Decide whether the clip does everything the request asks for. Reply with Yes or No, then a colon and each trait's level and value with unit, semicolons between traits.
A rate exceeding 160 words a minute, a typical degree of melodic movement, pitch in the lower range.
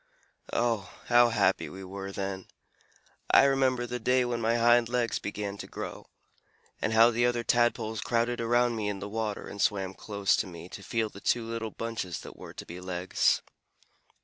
Yes: average, 185 wpm; average, 3.3 semitones; low, 115 Hz